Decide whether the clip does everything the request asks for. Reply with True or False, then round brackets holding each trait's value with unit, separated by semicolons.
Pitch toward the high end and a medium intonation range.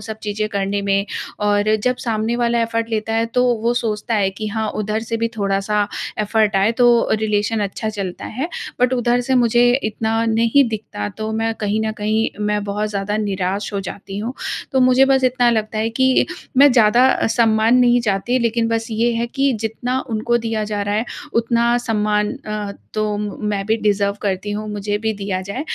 False (220 Hz; 2.1 semitones)